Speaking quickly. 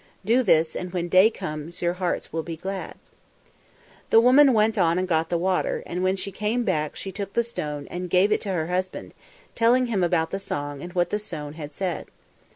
Yes: fast, 215 wpm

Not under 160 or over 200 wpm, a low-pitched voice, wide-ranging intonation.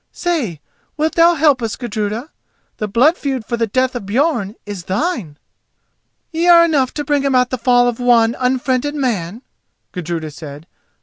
No: average, 165 wpm; high, 245 Hz; wide, 5.7 semitones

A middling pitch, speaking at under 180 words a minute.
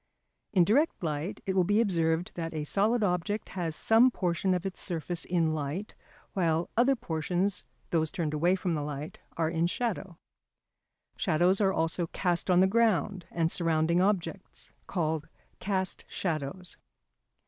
Yes: medium, 175 Hz; average, 150 wpm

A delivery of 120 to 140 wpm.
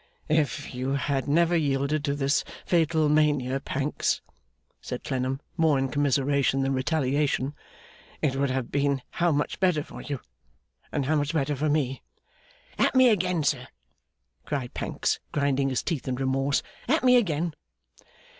No: average, 150 wpm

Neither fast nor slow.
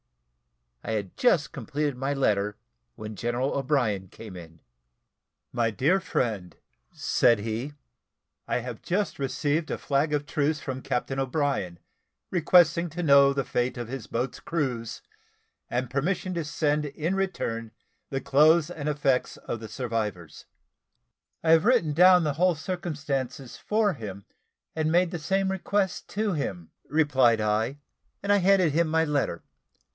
Yes: average, 145 wpm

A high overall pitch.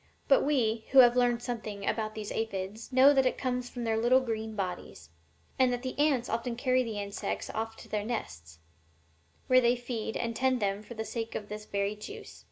Yes: high, 230 Hz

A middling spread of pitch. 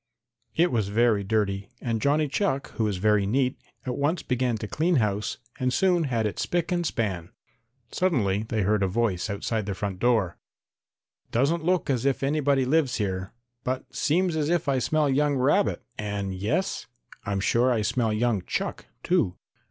No: wide, 5.8 semitones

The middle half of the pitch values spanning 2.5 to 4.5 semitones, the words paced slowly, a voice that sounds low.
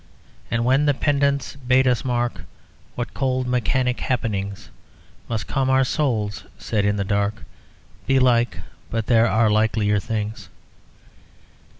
Yes: average, 3.6 semitones; slow, 125 wpm; low, 120 Hz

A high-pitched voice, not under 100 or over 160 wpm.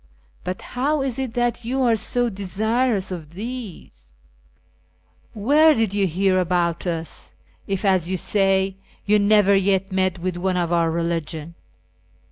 Yes: high, 195 Hz; average, 145 wpm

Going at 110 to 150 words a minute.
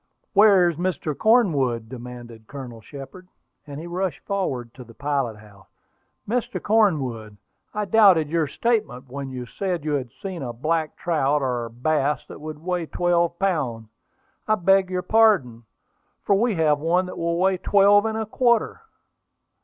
No: average, 160 wpm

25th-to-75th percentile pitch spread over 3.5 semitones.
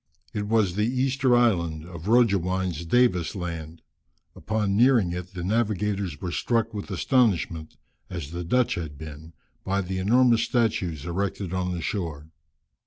Yes: average, 4.7 semitones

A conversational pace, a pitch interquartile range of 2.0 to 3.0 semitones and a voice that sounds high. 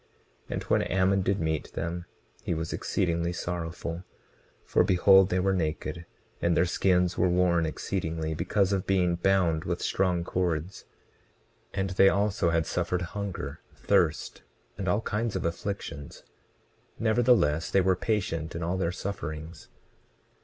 No: average, 145 wpm; narrow, 2.6 semitones; very low, 90 Hz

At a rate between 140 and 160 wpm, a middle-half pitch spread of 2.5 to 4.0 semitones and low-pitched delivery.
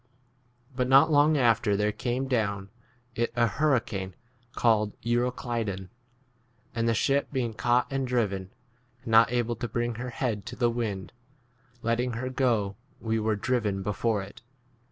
Yes: average, 155 wpm; average, 3.0 semitones; low, 115 Hz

